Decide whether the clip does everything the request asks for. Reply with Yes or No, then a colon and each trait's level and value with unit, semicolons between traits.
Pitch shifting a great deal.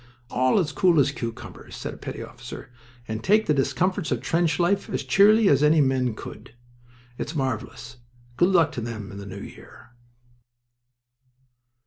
Yes: wide, 6.3 semitones